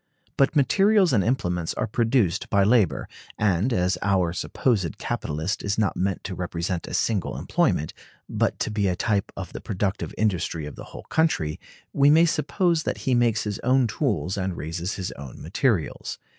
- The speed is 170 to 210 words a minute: Yes, average, 175 wpm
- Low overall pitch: Yes, low, 100 Hz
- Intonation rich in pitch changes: Yes, wide, 5.8 semitones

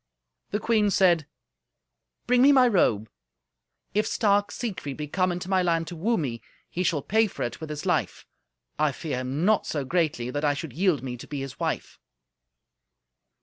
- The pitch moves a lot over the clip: Yes, wide, 6.0 semitones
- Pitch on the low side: No, medium, 165 Hz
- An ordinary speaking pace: Yes, average, 185 wpm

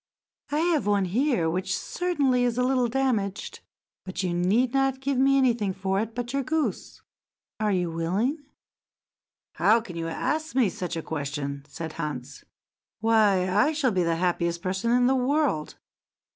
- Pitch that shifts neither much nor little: No, wide, 6.9 semitones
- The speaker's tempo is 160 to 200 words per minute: Yes, average, 165 wpm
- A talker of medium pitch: No, high, 215 Hz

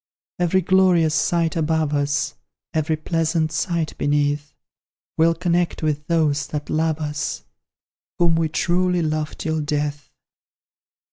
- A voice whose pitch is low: No, medium, 160 Hz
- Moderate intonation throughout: No, narrow, 2.0 semitones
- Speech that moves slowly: Yes, slow, 120 wpm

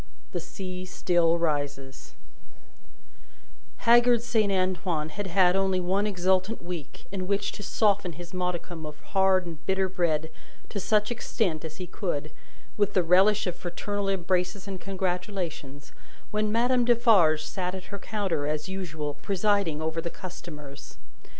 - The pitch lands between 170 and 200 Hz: Yes, medium, 185 Hz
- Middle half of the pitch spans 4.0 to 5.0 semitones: No, average, 3.3 semitones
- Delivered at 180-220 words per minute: No, average, 145 wpm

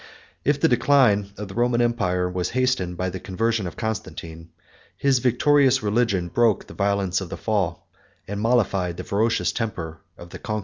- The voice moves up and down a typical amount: Yes, average, 4.6 semitones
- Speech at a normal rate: Yes, average, 175 wpm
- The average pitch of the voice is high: No, low, 105 Hz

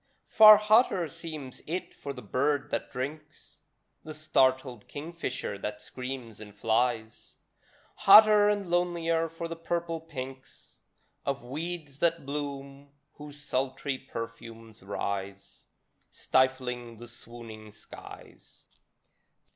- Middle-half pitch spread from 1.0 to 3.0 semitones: No, wide, 5.4 semitones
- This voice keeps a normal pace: No, slow, 105 wpm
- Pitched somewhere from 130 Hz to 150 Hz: Yes, medium, 140 Hz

